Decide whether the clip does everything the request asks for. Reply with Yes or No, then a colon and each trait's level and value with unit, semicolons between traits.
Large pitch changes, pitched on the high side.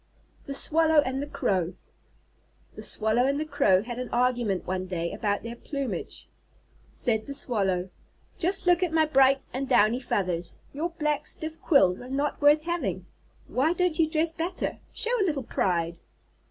Yes: wide, 6.9 semitones; very high, 270 Hz